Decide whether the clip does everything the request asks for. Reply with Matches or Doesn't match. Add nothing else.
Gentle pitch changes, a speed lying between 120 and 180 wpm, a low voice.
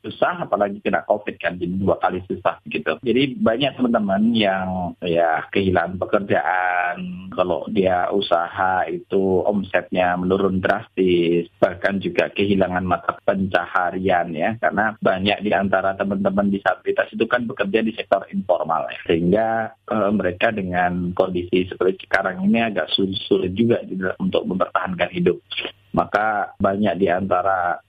Matches